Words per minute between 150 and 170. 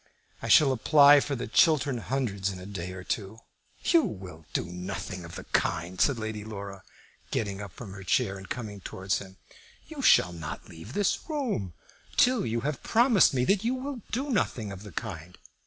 No: average, 190 wpm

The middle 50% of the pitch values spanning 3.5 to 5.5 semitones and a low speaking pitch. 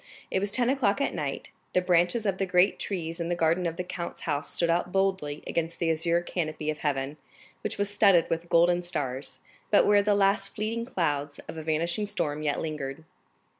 No: average, 4.0 semitones; medium, 170 Hz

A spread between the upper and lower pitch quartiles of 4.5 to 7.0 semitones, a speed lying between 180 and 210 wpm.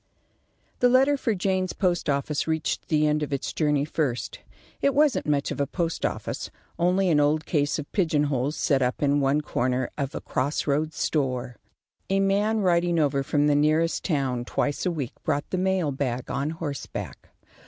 No: average, 3.9 semitones; average, 185 wpm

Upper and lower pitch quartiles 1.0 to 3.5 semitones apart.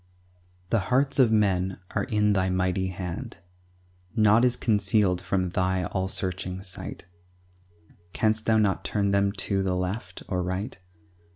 Yes: narrow, 2.6 semitones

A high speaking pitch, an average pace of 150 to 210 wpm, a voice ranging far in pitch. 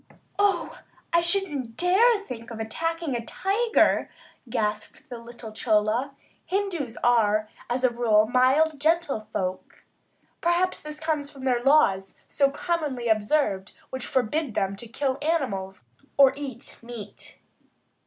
No: very high, 260 Hz; average, 140 wpm; wide, 6.2 semitones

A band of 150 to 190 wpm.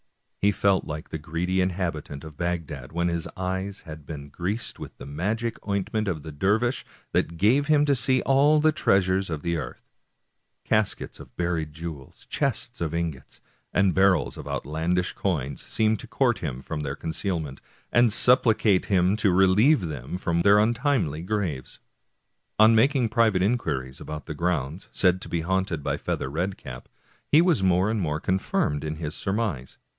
Yes: average, 170 wpm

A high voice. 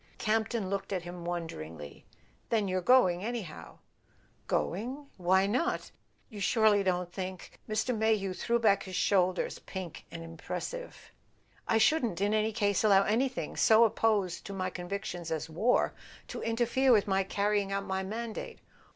Yes: high, 200 Hz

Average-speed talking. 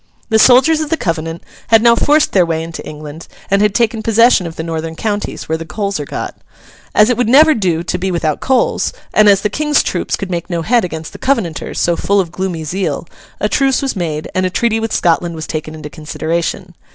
No: fast, 225 wpm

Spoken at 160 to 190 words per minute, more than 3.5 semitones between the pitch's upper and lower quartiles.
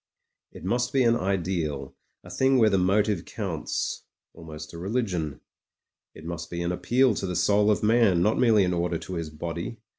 Yes: average, 185 wpm; average, 4.4 semitones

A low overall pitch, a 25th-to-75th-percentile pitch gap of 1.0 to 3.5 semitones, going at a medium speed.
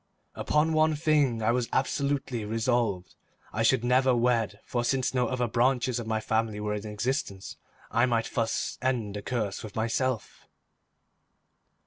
Yes: low, 120 Hz; average, 2.7 semitones; average, 150 wpm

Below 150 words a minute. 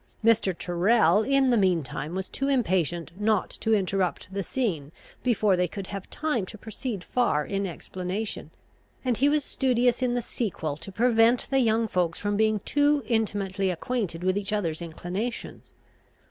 No: average, 165 wpm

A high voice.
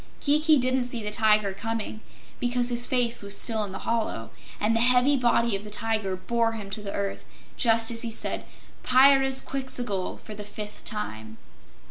Yes: high, 225 Hz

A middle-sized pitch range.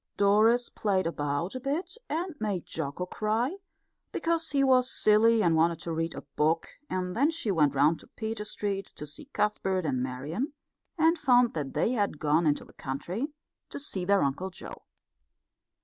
No: wide, 7.3 semitones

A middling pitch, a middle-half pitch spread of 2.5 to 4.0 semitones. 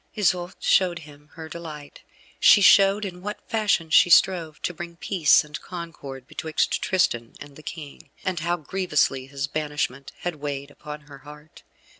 Yes: medium, 155 Hz; average, 3.5 semitones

